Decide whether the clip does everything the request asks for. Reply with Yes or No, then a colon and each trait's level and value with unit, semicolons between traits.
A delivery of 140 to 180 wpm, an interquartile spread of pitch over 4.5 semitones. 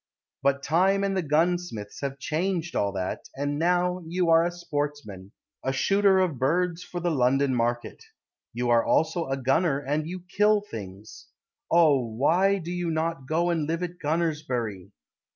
Yes: average, 170 wpm; average, 4.9 semitones